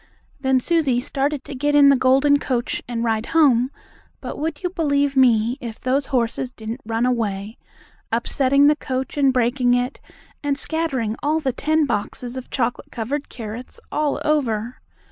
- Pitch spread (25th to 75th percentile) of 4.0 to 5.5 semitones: No, average, 3.3 semitones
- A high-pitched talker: Yes, very high, 260 Hz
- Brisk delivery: No, average, 165 wpm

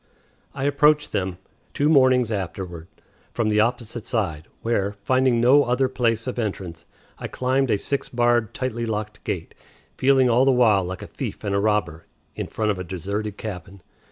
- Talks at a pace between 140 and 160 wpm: No, average, 175 wpm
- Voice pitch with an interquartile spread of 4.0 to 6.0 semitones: Yes, average, 4.4 semitones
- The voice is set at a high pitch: No, low, 110 Hz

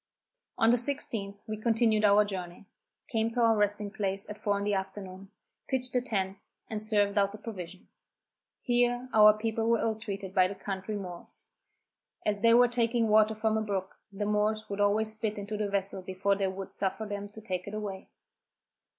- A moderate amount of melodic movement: No, narrow, 1.9 semitones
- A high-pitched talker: Yes, high, 210 Hz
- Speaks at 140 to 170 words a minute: No, average, 190 wpm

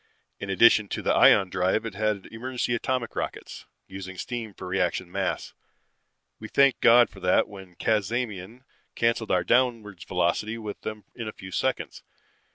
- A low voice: Yes, low, 105 Hz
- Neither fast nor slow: Yes, average, 160 wpm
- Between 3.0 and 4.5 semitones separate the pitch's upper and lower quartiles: Yes, average, 3.7 semitones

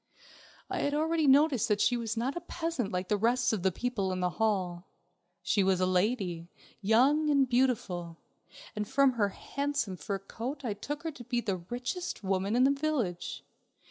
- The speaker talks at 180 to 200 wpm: Yes, average, 185 wpm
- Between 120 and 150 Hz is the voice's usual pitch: No, high, 230 Hz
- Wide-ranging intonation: Yes, wide, 6.4 semitones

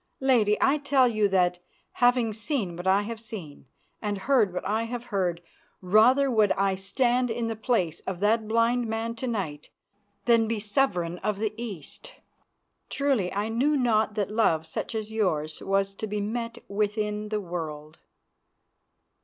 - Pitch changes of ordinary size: Yes, average, 3.3 semitones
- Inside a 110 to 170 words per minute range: Yes, average, 165 wpm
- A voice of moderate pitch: No, high, 215 Hz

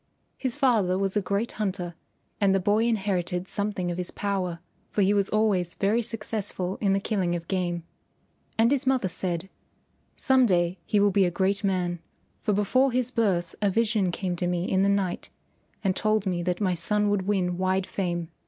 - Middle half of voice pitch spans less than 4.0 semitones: Yes, average, 2.7 semitones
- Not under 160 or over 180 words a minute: No, average, 190 wpm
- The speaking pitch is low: No, high, 195 Hz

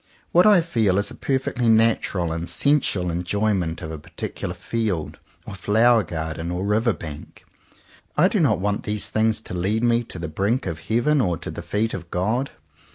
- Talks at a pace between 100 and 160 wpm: No, average, 185 wpm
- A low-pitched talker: Yes, low, 105 Hz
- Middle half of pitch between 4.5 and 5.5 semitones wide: Yes, average, 4.9 semitones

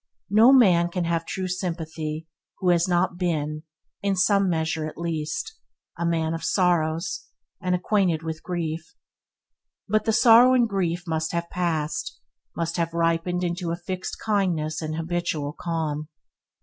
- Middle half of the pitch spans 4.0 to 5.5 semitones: No, narrow, 2.4 semitones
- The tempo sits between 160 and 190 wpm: No, average, 150 wpm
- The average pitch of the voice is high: No, medium, 170 Hz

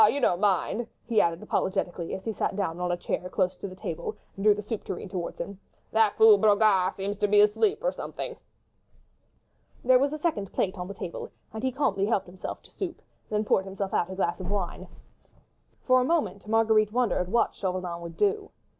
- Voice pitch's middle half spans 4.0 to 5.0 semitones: No, average, 3.2 semitones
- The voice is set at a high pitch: Yes, high, 200 Hz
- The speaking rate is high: Yes, fast, 210 wpm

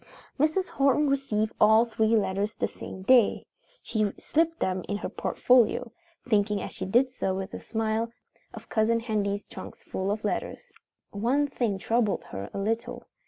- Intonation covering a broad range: No, average, 3.4 semitones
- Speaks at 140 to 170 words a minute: Yes, average, 165 wpm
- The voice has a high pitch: Yes, high, 220 Hz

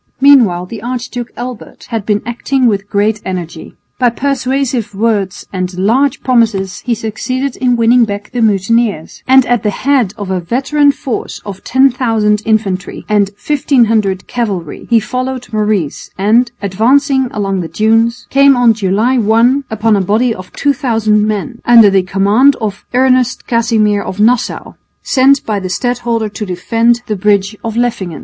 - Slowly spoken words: No, average, 155 wpm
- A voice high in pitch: Yes, high, 225 Hz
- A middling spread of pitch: Yes, average, 3.6 semitones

